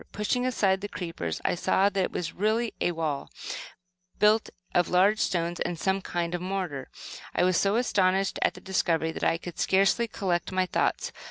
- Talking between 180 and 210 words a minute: Yes, average, 185 wpm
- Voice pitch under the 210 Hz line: Yes, medium, 185 Hz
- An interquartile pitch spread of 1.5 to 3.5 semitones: Yes, narrow, 2.6 semitones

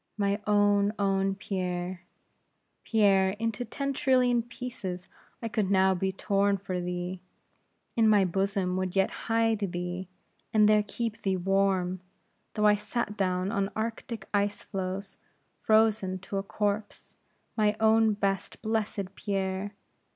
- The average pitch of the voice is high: Yes, high, 200 Hz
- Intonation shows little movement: Yes, narrow, 2.3 semitones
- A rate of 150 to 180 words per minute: No, slow, 135 wpm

